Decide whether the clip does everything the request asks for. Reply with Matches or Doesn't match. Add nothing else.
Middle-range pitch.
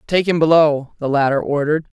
Matches